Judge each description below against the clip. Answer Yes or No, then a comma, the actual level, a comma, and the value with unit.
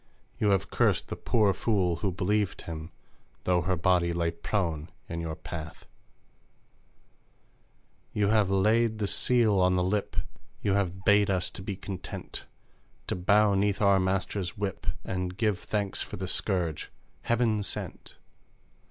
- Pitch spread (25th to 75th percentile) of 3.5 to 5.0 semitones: No, narrow, 2.5 semitones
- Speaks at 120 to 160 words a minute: Yes, average, 145 wpm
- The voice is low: Yes, very low, 95 Hz